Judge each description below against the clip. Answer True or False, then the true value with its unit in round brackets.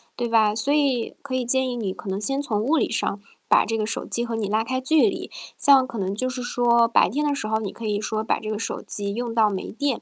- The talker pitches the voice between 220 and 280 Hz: True (230 Hz)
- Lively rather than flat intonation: False (3.3 semitones)